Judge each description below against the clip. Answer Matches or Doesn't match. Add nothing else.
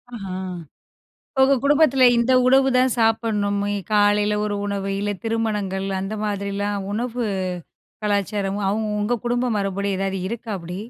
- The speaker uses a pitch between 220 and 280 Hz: Doesn't match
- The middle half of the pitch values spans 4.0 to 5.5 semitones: Doesn't match